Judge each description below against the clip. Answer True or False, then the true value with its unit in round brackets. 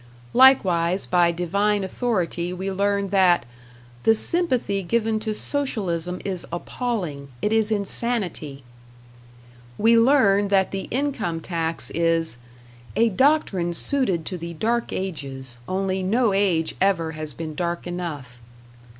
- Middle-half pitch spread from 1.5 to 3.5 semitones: False (4.5 semitones)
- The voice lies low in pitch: False (190 Hz)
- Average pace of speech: False (125 wpm)